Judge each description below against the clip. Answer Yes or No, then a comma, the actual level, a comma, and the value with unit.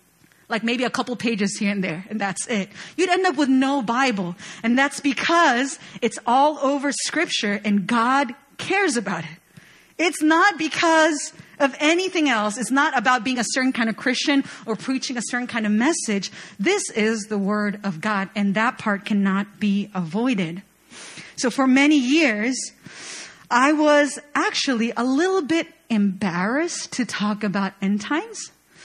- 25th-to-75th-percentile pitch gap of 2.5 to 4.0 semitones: No, wide, 5.6 semitones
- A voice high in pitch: Yes, high, 245 Hz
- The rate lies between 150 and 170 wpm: Yes, average, 165 wpm